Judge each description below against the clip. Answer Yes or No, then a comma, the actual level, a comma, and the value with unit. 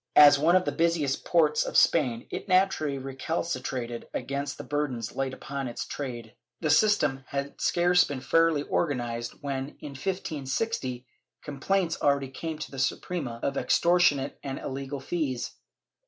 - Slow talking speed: No, average, 145 wpm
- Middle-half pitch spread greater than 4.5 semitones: No, average, 3.8 semitones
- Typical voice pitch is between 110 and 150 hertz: Yes, medium, 140 Hz